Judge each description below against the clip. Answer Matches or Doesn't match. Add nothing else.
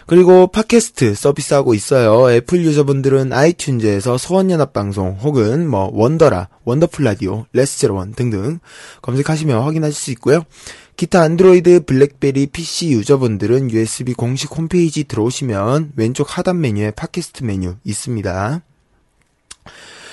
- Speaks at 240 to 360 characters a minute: Matches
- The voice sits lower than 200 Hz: Matches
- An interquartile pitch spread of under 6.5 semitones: Matches